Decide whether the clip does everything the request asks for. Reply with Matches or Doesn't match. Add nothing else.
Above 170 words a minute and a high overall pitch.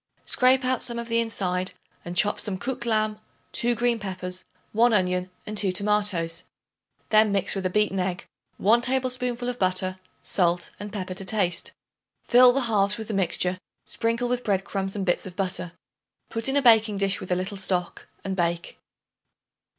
Matches